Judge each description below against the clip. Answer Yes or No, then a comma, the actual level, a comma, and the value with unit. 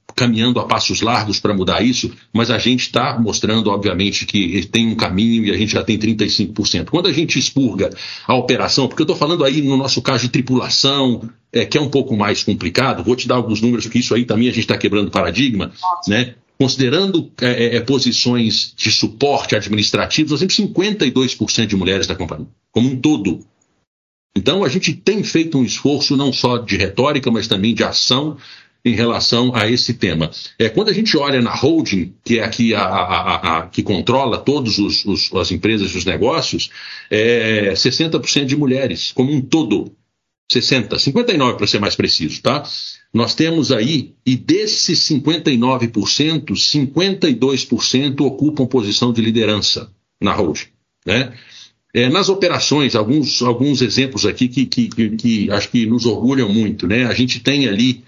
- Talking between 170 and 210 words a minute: Yes, average, 175 wpm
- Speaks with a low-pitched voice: Yes, low, 120 Hz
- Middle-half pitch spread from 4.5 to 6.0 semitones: No, average, 3.8 semitones